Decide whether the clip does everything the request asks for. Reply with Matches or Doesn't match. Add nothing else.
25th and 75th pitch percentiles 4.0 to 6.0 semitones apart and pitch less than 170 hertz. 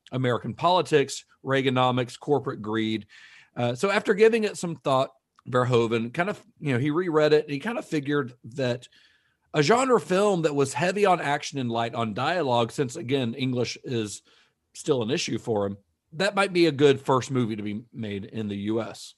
Matches